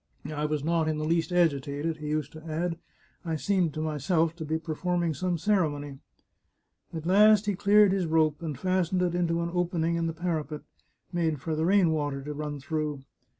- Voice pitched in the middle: Yes, medium, 160 Hz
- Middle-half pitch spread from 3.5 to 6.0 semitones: No, narrow, 2.6 semitones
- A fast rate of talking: Yes, fast, 215 wpm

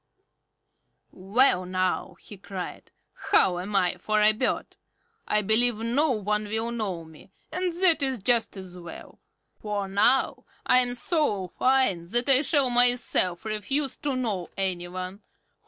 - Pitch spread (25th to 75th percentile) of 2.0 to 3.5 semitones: No, average, 5.1 semitones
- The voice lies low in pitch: No, high, 215 Hz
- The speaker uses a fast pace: No, average, 145 wpm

